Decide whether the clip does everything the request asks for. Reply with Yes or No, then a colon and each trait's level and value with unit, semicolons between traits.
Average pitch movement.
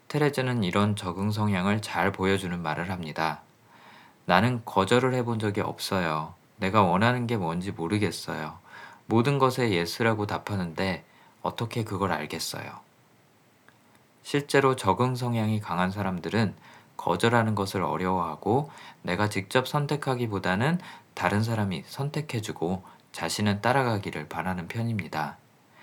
Yes: average, 4.9 semitones